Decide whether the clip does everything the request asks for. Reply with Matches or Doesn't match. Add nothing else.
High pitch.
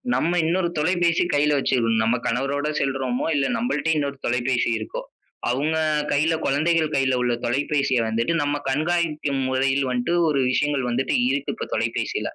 Doesn't match